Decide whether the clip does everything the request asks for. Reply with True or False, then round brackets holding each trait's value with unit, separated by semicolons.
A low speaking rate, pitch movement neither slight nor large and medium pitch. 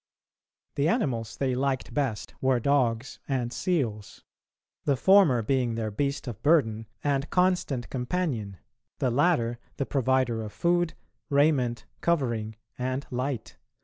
False (125 wpm; 3.6 semitones; 130 Hz)